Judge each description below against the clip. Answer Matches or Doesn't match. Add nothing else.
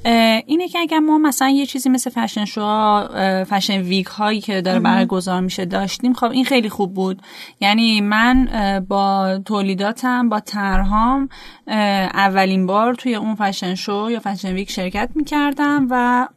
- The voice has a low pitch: Doesn't match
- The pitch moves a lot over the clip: Doesn't match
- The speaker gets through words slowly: Doesn't match